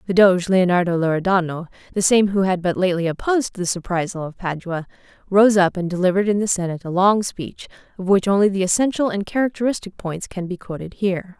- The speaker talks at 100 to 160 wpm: No, average, 195 wpm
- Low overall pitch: No, high, 190 Hz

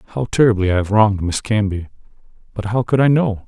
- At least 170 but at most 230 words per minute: Yes, fast, 205 wpm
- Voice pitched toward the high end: No, low, 110 Hz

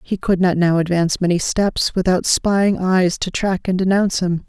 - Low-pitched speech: No, medium, 185 Hz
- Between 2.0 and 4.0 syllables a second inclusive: No, 4.8 syllables/s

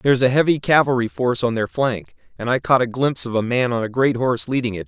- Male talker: Yes, male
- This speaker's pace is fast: Yes, fast, 270 wpm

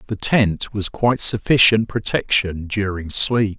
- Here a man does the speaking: Yes, male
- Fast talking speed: No, slow, 135 wpm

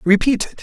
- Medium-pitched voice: No, high, 220 Hz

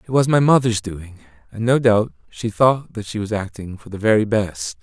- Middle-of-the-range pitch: No, low, 105 Hz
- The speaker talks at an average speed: No, fast, 225 wpm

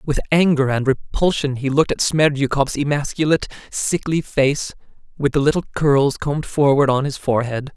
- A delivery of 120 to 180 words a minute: Yes, average, 155 wpm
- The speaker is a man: Yes, male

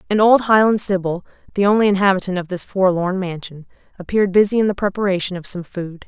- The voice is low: No, high, 190 Hz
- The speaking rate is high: No, average, 190 wpm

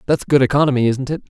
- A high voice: No, low, 135 Hz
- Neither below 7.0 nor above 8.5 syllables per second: Yes, 7.3 syllables/s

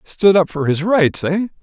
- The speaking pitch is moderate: Yes, medium, 175 Hz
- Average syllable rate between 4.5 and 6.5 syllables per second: No, 4.3 syllables/s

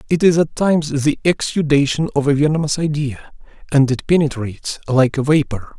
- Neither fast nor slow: Yes, average, 165 wpm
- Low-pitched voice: No, medium, 145 Hz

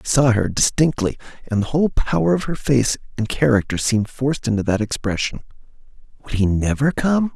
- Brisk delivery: No, average, 170 wpm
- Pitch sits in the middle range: No, low, 125 Hz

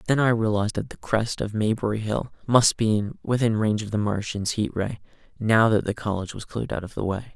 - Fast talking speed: Yes, fast, 230 wpm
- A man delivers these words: Yes, male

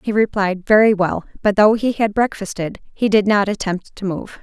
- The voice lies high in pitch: Yes, high, 205 Hz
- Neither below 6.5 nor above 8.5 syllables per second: No, 5.0 syllables/s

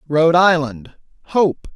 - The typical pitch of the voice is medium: Yes, medium, 160 Hz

